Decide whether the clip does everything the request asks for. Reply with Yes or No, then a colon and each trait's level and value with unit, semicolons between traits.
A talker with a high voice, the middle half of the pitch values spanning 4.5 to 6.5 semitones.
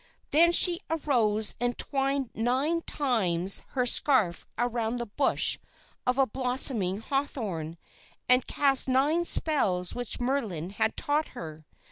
Yes: high, 245 Hz; average, 5.0 semitones